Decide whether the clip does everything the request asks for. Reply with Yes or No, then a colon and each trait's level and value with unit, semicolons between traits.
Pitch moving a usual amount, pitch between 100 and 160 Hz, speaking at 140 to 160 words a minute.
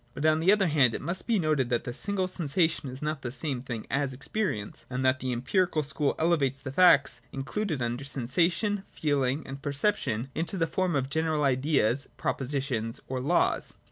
No: average, 4.3 semitones; medium, 140 Hz; average, 185 wpm